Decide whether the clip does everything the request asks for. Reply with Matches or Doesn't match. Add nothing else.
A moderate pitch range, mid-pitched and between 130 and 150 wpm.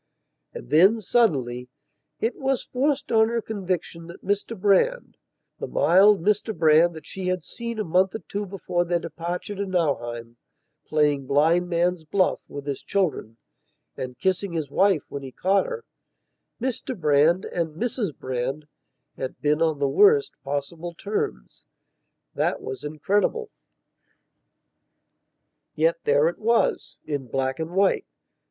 Doesn't match